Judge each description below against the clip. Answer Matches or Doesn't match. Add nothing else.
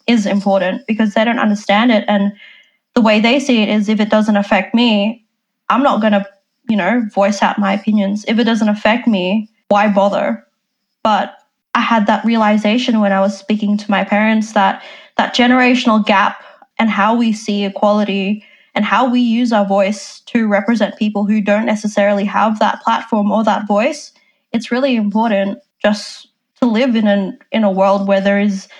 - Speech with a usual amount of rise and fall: Doesn't match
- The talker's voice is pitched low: Doesn't match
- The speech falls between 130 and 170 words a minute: Doesn't match